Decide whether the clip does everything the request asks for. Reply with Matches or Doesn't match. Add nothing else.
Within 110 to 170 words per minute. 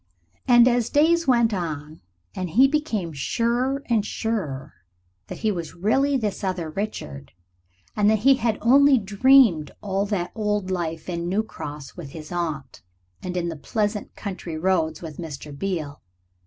Matches